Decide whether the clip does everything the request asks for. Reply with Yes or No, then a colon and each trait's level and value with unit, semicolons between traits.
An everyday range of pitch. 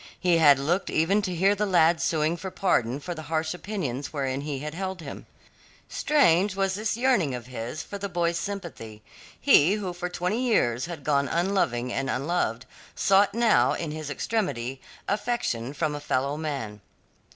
No: wide, 5.7 semitones